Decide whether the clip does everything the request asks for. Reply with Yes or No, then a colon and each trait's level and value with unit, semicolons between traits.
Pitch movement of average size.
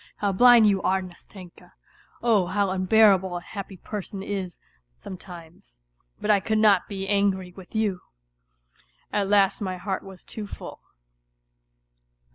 No: narrow, 1.9 semitones